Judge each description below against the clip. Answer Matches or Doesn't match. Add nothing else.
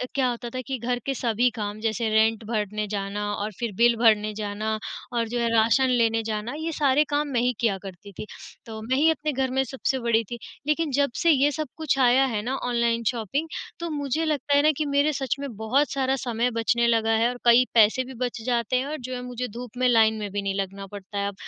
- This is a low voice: Doesn't match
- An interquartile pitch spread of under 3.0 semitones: Doesn't match